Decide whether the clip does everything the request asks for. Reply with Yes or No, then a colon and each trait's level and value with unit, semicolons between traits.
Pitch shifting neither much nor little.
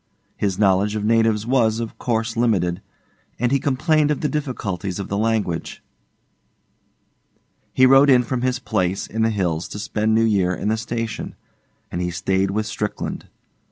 Yes: average, 3.8 semitones